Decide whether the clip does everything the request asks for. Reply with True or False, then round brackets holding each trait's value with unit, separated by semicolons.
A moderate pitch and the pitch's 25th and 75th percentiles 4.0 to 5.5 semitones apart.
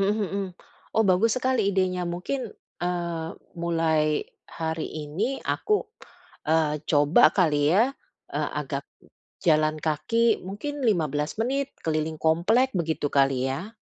True (170 Hz; 5.2 semitones)